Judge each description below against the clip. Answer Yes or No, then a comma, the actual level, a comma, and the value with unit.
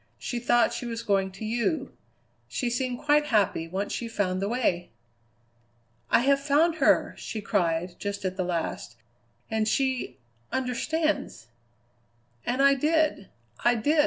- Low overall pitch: No, high, 235 Hz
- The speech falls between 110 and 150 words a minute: Yes, average, 145 wpm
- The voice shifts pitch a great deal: Yes, wide, 5.8 semitones